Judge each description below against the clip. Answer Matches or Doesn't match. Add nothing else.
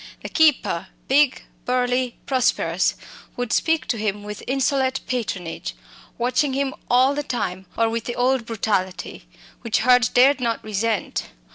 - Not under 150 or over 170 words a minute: Doesn't match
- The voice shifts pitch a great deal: Doesn't match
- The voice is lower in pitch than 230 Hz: Doesn't match